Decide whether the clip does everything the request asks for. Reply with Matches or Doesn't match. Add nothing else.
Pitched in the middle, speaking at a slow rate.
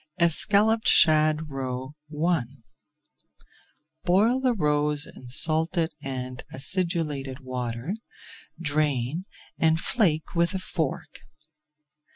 Matches